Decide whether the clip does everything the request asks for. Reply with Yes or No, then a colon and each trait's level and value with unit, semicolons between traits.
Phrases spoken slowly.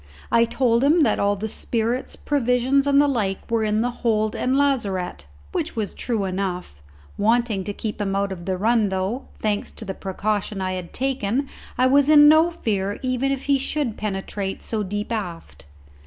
No: average, 185 wpm